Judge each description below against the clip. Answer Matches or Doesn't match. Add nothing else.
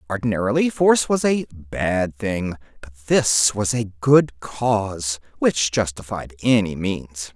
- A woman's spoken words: Doesn't match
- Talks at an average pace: Doesn't match